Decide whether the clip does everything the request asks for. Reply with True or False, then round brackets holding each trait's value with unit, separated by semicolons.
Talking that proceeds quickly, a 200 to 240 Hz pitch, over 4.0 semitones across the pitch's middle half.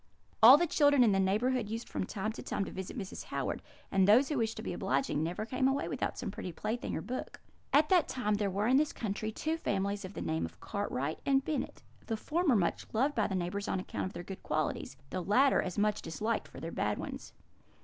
True (235 wpm; 215 Hz; 5.3 semitones)